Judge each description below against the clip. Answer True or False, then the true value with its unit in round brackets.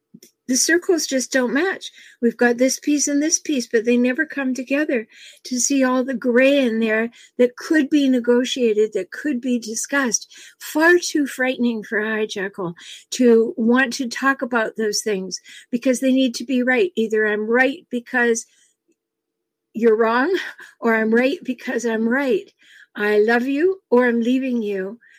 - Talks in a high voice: True (250 Hz)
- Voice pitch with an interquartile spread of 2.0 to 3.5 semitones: True (3.0 semitones)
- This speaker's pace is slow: False (165 wpm)